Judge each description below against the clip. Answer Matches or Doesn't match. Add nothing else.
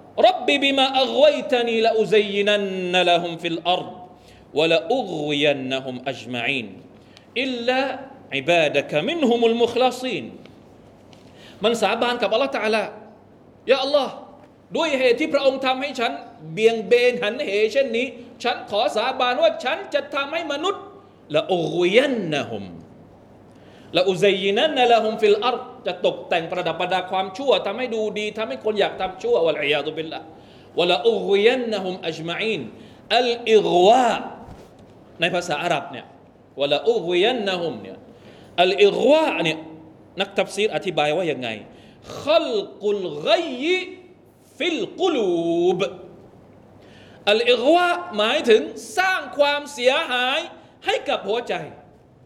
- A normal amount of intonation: Doesn't match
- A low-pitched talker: Doesn't match